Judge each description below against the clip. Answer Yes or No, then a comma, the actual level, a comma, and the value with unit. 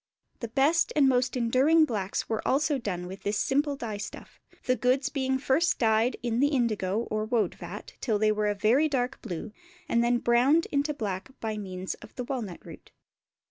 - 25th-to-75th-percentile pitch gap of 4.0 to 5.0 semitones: Yes, average, 4.3 semitones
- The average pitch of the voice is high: Yes, high, 240 Hz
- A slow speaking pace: No, average, 190 wpm